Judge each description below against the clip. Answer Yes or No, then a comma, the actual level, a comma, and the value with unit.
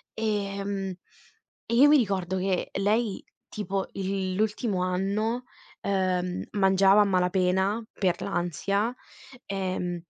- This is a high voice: Yes, high, 195 Hz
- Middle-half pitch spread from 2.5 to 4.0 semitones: No, narrow, 2.1 semitones